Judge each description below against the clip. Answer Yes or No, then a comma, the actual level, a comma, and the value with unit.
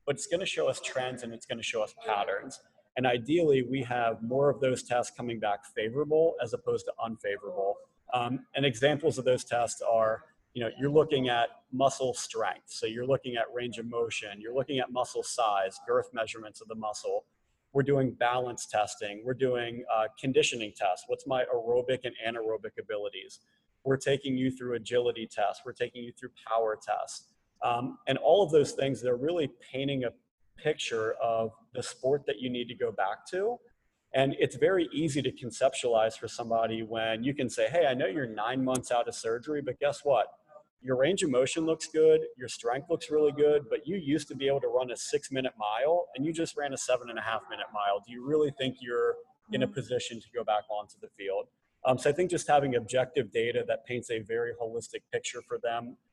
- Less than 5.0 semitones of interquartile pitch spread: No, wide, 5.5 semitones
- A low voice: Yes, low, 130 Hz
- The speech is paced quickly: Yes, fast, 210 wpm